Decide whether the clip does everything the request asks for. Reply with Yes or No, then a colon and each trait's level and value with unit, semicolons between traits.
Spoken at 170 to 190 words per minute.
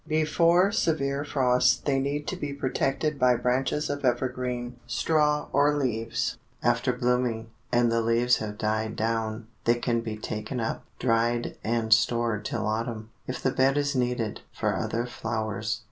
No: average, 155 wpm